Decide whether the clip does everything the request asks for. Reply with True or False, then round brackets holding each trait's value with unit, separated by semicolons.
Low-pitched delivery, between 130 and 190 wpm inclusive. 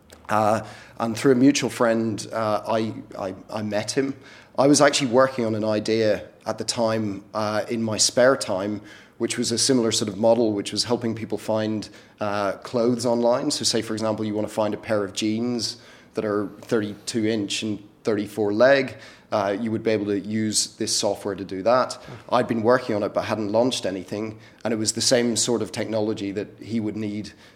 False (110 Hz; 205 wpm)